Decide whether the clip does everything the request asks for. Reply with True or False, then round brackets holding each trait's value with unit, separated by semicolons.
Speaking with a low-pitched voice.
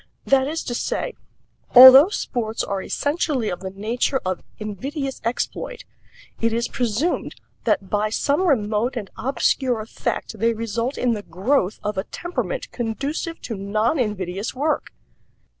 False (235 Hz)